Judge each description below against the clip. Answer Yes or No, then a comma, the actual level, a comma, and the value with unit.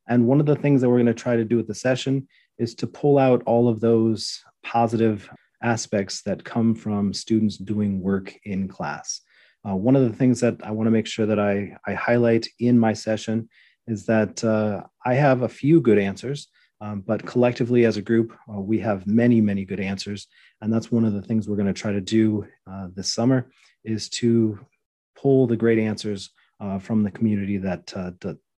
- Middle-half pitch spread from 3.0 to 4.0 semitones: No, narrow, 2.5 semitones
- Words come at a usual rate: No, fast, 210 wpm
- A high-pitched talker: No, low, 110 Hz